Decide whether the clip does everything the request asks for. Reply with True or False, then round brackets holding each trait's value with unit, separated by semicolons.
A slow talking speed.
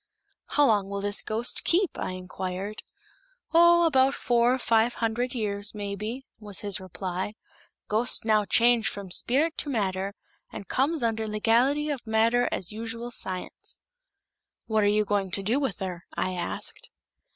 False (150 wpm)